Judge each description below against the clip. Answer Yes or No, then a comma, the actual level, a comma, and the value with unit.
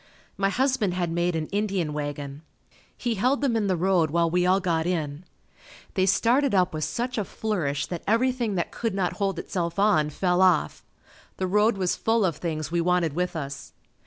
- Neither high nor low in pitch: Yes, medium, 180 Hz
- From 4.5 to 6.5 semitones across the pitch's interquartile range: No, average, 4.1 semitones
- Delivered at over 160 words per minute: Yes, average, 190 wpm